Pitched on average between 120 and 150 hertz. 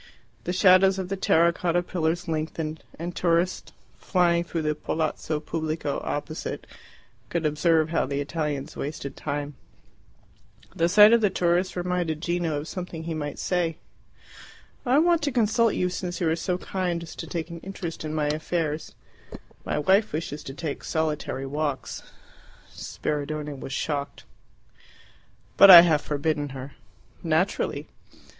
No: medium, 165 Hz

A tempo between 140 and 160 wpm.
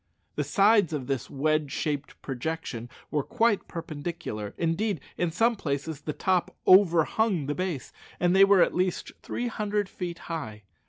Yes: average, 155 wpm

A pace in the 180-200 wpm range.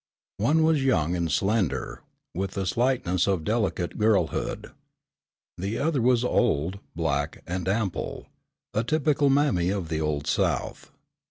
No: slow, 135 wpm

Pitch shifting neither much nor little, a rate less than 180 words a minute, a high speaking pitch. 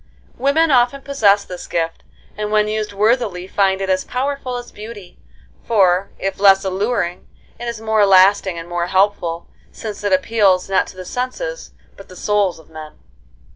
Yes: average, 3.7 semitones; average, 170 wpm; high, 200 Hz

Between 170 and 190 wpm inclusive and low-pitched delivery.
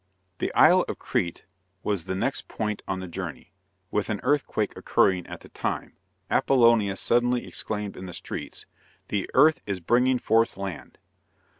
No: average, 155 wpm; low, 105 Hz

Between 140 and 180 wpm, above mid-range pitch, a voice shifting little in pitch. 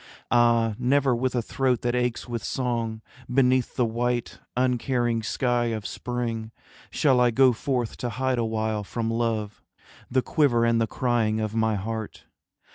No: average, 155 wpm; low, 120 Hz; narrow, 1.8 semitones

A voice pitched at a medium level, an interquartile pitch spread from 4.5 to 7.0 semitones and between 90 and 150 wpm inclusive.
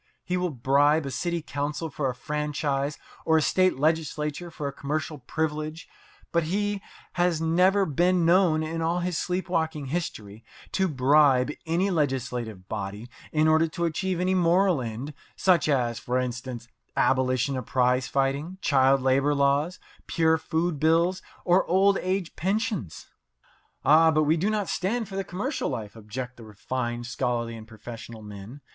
No: medium, 150 Hz; average, 5.2 semitones; average, 160 wpm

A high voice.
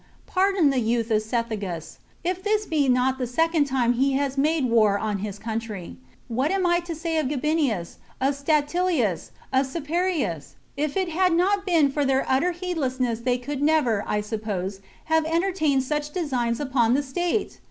Yes: very high, 275 Hz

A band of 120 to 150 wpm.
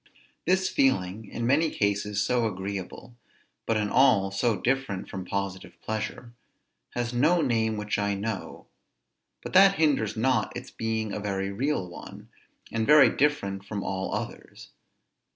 Yes: average, 145 wpm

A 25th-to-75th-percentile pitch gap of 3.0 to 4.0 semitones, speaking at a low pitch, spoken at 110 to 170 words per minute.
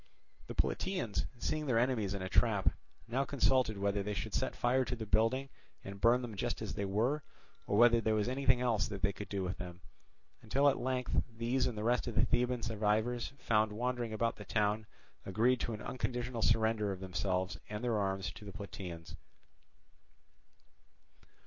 No: average, 3.3 semitones; low, 110 Hz; average, 185 wpm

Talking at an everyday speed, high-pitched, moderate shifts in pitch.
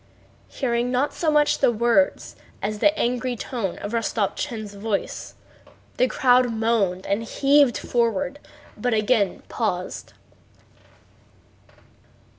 No: slow, 105 wpm; high, 235 Hz; average, 3.2 semitones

